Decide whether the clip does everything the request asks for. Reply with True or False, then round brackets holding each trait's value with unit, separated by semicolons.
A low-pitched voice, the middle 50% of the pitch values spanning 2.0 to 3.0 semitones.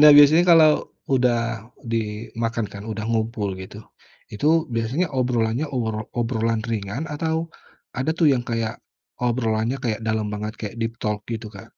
True (115 Hz; 2.5 semitones)